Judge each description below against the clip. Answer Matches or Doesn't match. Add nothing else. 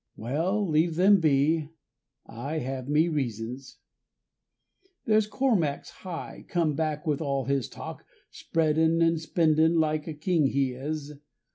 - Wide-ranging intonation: Doesn't match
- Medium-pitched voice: Matches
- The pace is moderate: Doesn't match